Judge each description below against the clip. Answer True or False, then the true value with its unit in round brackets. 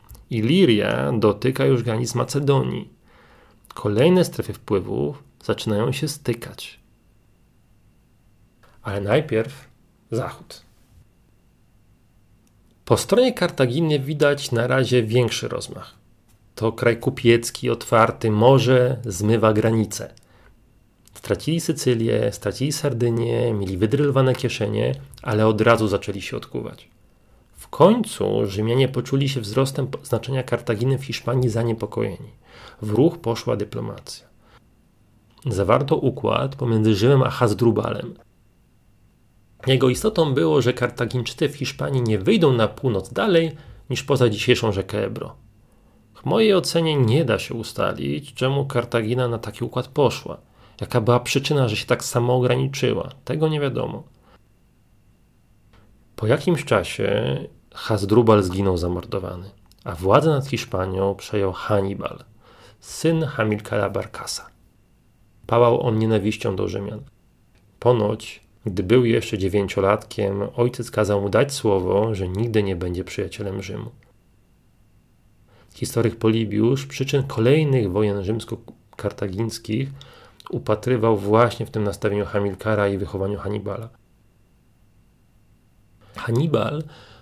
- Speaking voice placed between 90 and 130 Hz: True (115 Hz)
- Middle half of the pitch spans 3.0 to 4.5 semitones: True (3.3 semitones)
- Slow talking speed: True (105 wpm)